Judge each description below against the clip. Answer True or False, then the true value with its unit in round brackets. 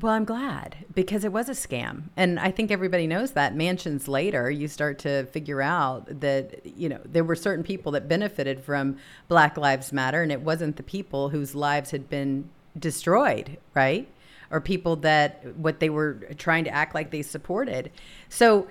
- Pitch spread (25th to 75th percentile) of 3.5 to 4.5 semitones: True (3.9 semitones)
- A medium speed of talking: True (185 wpm)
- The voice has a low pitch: False (155 Hz)